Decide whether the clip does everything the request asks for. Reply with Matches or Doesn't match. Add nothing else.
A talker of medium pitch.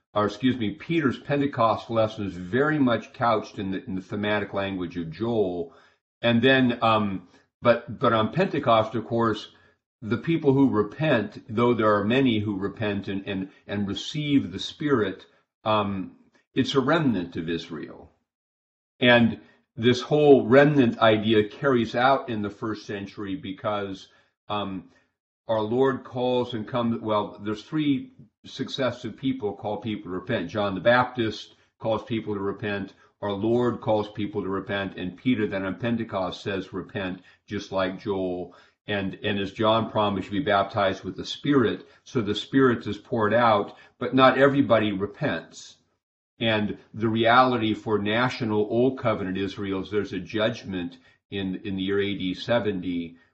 Doesn't match